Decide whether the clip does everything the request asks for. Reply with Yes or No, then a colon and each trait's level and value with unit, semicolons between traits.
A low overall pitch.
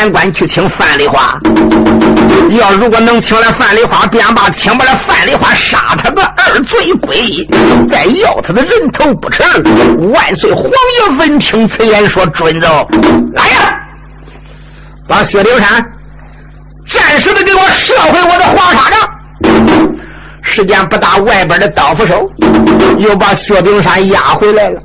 No: high, 220 Hz